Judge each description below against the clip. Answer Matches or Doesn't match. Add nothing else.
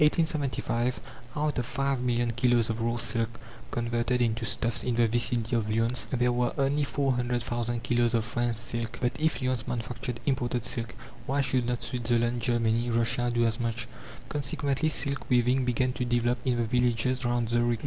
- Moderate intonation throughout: Doesn't match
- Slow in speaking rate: Doesn't match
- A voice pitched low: Matches